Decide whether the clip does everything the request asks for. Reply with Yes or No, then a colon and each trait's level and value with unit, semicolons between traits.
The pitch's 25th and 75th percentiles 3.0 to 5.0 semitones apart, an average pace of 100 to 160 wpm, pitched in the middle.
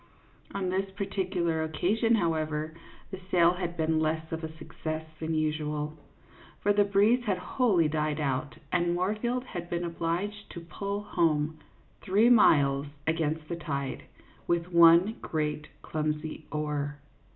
Yes: average, 3.7 semitones; average, 140 wpm; medium, 165 Hz